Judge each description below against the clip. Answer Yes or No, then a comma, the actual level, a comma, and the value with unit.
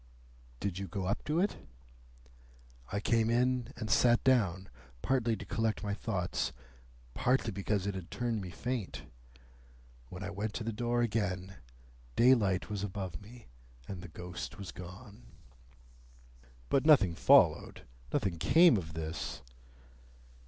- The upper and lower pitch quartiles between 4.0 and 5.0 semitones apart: Yes, average, 4.3 semitones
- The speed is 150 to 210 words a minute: No, average, 140 wpm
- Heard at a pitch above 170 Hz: No, low, 105 Hz